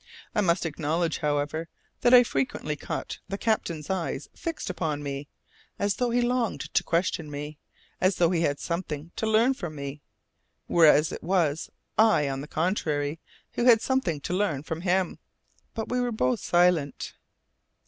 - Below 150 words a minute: No, average, 165 wpm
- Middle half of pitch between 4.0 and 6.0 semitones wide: Yes, wide, 5.6 semitones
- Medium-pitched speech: Yes, medium, 170 Hz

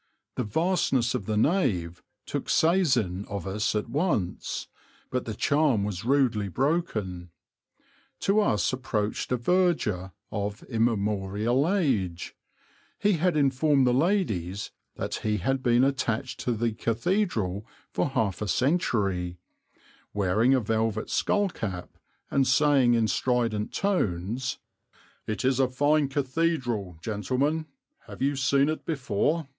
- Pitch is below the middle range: Yes, low, 120 Hz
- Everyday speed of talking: No, slow, 130 wpm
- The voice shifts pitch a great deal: Yes, wide, 5.7 semitones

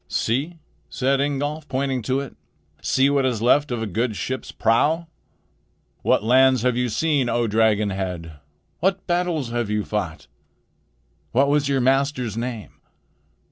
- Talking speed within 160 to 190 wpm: No, average, 145 wpm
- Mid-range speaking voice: No, low, 130 Hz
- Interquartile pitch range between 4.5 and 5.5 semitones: No, average, 3.9 semitones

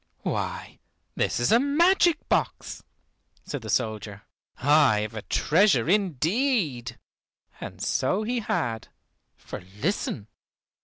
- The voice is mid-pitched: Yes, medium, 150 Hz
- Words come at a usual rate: No, slow, 110 wpm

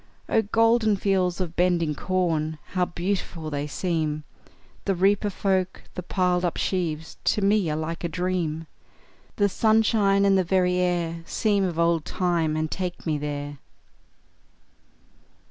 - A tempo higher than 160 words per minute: No, average, 145 wpm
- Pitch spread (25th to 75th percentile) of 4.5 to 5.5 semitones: No, average, 3.2 semitones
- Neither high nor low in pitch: Yes, medium, 180 Hz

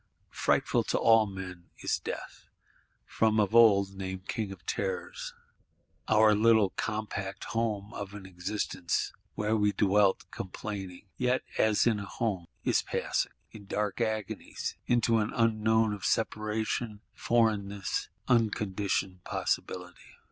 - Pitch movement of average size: No, narrow, 2.3 semitones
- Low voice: Yes, low, 105 Hz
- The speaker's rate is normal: No, slow, 125 wpm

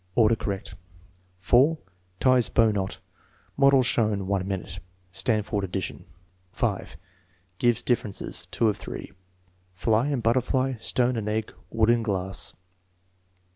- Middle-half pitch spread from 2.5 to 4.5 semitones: Yes, average, 3.8 semitones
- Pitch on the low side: Yes, low, 110 Hz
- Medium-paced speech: No, slow, 125 wpm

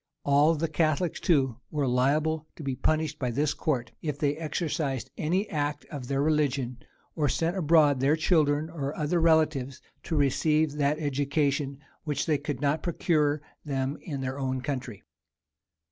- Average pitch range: No, narrow, 2.3 semitones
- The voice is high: No, medium, 145 Hz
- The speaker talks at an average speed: Yes, average, 160 wpm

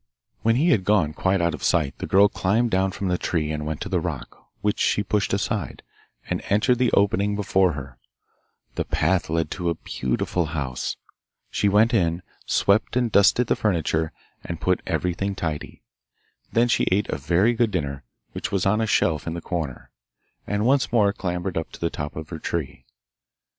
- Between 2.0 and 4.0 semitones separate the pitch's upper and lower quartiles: No, average, 4.4 semitones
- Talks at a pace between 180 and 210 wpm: Yes, average, 190 wpm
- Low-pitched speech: Yes, very low, 95 Hz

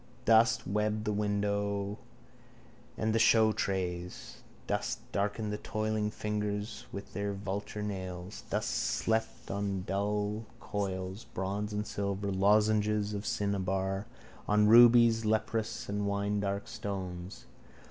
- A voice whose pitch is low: Yes, low, 105 Hz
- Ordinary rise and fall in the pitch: No, narrow, 1.3 semitones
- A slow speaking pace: Yes, slow, 115 wpm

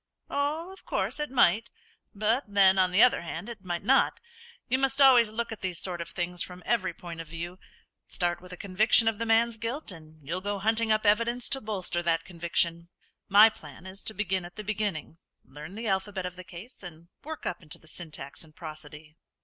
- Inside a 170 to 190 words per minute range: No, fast, 205 wpm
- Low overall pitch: No, high, 190 Hz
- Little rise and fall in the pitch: No, average, 4.7 semitones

